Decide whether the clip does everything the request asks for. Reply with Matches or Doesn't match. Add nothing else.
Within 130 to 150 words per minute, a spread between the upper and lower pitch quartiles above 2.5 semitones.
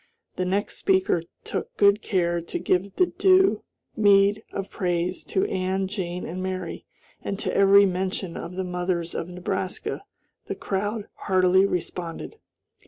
Doesn't match